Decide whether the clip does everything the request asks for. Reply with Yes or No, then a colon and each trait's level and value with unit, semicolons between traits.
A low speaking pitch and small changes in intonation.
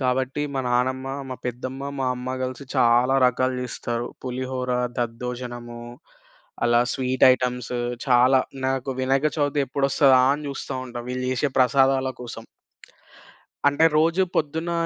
Yes: low, 130 Hz; narrow, 1.4 semitones